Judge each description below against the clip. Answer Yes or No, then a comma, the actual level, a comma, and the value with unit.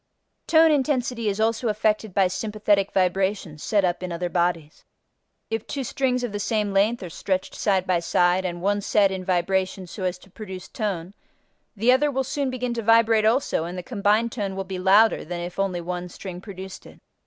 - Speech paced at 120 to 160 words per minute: No, average, 200 wpm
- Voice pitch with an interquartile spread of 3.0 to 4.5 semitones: Yes, average, 3.6 semitones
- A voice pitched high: Yes, high, 195 Hz